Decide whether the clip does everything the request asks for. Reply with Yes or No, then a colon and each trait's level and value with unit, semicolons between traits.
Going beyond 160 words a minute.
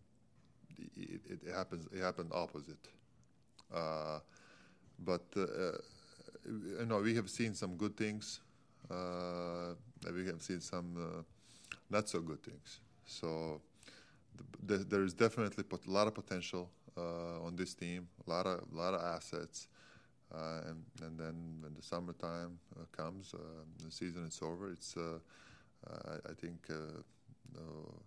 No: average, 150 wpm